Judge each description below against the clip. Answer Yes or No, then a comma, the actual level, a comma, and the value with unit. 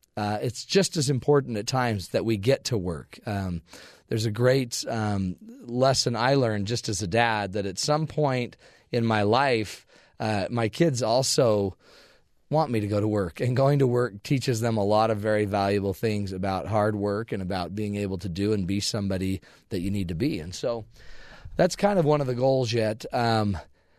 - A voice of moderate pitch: No, low, 110 Hz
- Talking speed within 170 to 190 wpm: No, fast, 205 wpm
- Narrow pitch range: No, average, 4.0 semitones